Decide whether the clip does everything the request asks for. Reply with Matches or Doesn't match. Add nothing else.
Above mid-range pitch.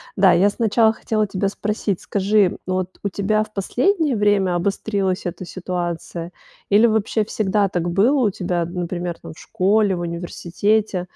Matches